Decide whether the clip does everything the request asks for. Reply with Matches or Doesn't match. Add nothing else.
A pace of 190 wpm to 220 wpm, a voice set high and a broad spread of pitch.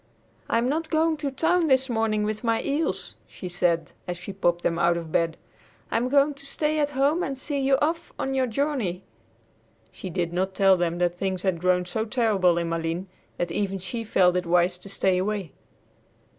Matches